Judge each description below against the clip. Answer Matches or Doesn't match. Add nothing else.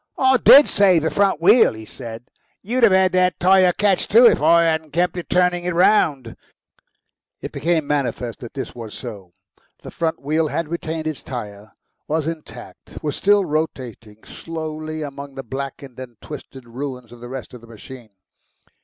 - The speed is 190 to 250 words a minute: Doesn't match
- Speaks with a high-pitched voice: Doesn't match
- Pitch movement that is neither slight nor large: Doesn't match